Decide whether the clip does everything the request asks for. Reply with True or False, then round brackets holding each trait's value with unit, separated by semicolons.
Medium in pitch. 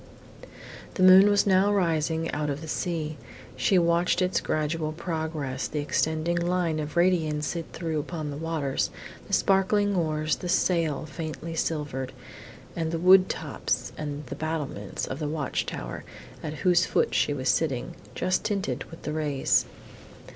True (160 Hz)